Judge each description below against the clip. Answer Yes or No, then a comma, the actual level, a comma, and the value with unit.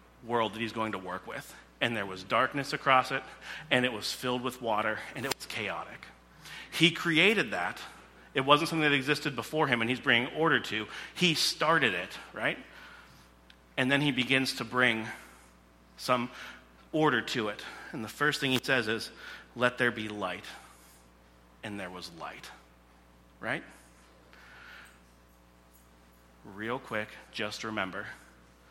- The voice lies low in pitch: Yes, low, 110 Hz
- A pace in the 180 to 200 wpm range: No, average, 150 wpm